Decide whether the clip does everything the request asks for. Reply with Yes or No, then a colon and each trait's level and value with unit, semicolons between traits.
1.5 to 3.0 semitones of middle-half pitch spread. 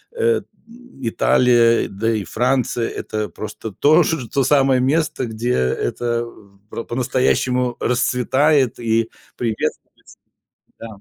Yes: average, 2.7 semitones